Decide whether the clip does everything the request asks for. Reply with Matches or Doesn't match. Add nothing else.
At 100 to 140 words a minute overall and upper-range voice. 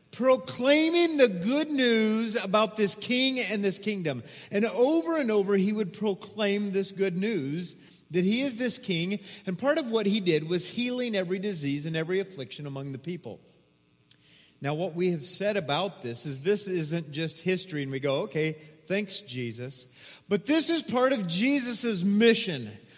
Doesn't match